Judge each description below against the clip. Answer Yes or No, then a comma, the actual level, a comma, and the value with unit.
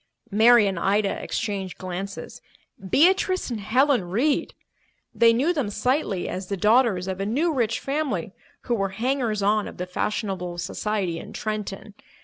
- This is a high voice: Yes, high, 210 Hz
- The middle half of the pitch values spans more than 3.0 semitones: Yes, average, 4.4 semitones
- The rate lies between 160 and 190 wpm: No, average, 150 wpm